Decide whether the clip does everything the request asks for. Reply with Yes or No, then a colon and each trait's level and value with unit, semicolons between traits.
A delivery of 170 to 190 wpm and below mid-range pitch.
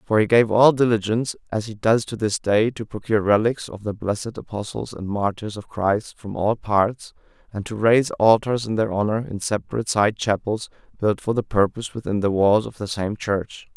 No: fast, 205 wpm; low, 110 Hz